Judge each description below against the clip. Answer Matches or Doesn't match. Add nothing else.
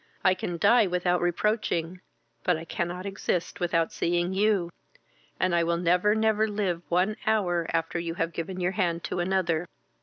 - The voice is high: Doesn't match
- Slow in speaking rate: Doesn't match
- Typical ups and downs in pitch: Doesn't match